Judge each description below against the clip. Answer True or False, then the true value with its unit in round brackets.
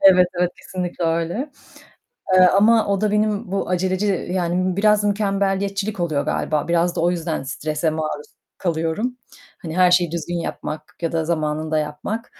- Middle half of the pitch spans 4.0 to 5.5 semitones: False (3.5 semitones)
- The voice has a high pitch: False (180 Hz)